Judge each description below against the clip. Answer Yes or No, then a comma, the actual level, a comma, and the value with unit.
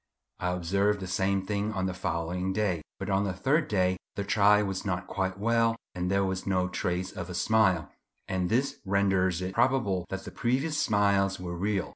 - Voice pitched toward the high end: No, very low, 95 Hz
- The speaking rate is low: No, average, 195 wpm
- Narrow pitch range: Yes, narrow, 2.1 semitones